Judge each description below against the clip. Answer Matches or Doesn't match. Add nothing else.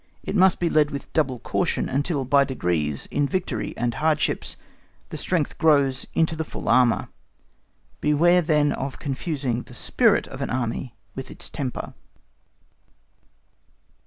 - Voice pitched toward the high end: Doesn't match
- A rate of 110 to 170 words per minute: Matches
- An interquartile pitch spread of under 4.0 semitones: Matches